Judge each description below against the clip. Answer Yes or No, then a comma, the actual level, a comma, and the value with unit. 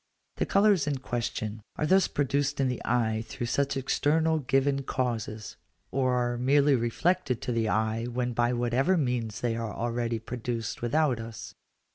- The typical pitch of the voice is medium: No, low, 125 Hz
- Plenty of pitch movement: No, average, 3.3 semitones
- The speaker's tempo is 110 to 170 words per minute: Yes, average, 160 wpm